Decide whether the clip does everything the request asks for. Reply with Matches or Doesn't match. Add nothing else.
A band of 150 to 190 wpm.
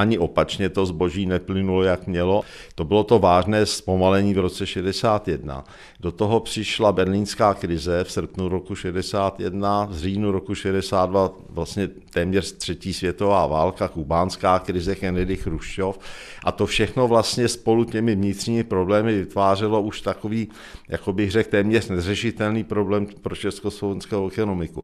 Doesn't match